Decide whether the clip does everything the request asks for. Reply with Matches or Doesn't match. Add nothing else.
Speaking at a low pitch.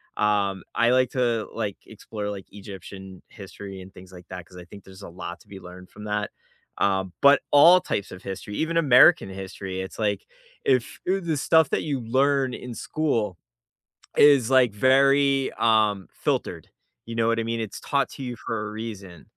Matches